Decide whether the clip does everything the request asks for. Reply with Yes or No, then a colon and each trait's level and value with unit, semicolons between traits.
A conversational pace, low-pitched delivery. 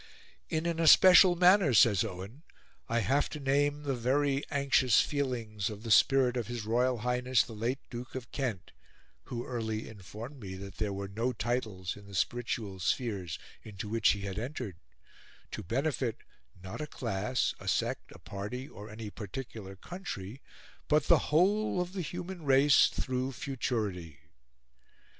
Yes: average, 155 wpm; low, 120 Hz